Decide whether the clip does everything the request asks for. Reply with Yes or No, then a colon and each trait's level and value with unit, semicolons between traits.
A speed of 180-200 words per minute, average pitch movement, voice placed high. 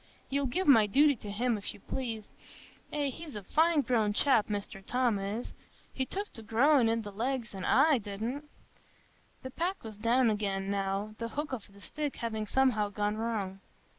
Yes: average, 185 wpm; average, 4.6 semitones; high, 230 Hz